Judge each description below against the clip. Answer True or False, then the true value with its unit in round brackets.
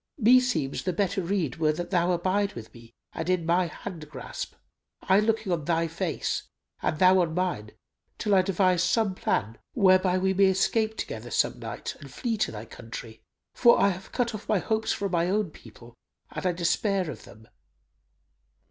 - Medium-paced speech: True (185 wpm)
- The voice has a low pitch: False (185 Hz)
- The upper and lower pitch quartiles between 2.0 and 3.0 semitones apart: False (3.7 semitones)